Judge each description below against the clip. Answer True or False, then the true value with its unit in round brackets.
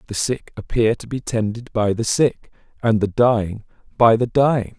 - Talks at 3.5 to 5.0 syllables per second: True (4.8 syllables/s)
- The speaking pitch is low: True (115 Hz)